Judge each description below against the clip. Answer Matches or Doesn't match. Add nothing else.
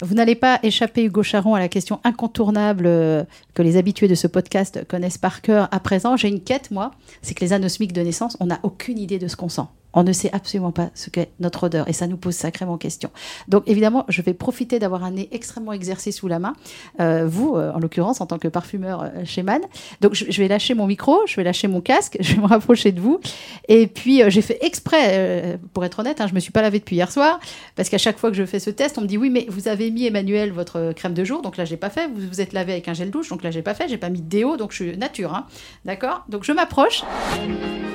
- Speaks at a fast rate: Matches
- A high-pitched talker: Matches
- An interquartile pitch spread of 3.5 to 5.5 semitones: Matches